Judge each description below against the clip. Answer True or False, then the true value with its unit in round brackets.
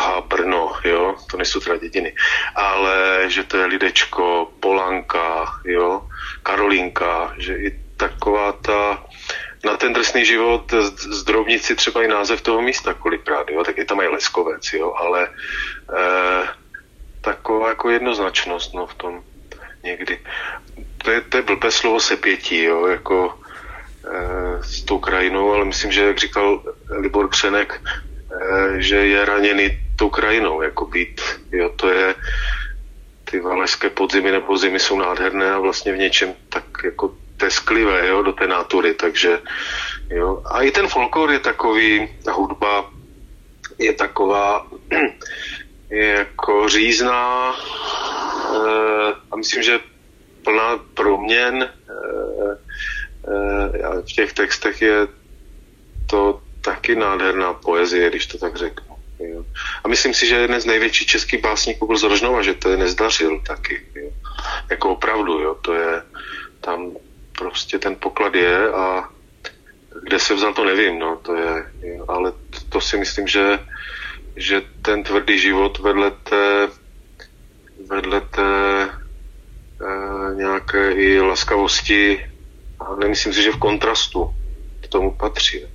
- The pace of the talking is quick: False (135 wpm)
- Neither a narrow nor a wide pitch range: True (3.2 semitones)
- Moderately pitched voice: False (100 Hz)